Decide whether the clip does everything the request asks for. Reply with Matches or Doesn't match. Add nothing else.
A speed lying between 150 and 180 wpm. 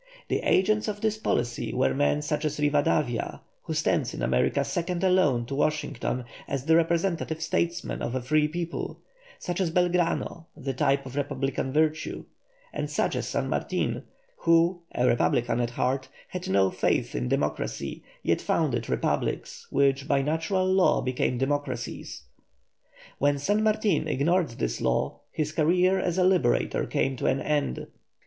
Matches